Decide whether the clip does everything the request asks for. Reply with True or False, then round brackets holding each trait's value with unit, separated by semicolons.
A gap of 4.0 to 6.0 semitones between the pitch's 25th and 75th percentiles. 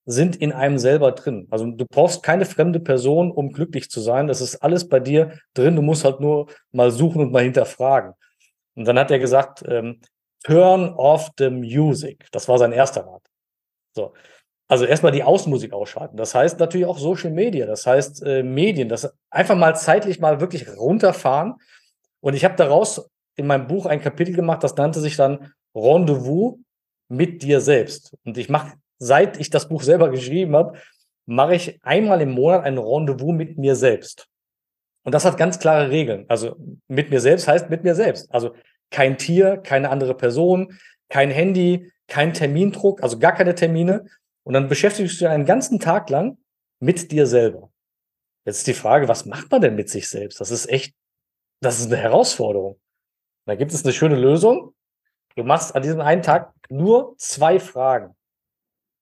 True (4.6 semitones)